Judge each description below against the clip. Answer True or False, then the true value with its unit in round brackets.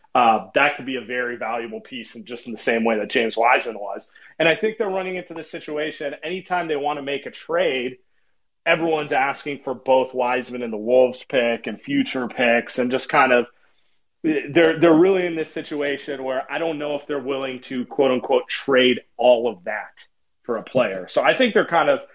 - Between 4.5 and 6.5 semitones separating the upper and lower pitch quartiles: True (4.8 semitones)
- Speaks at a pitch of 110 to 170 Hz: True (140 Hz)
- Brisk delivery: True (210 wpm)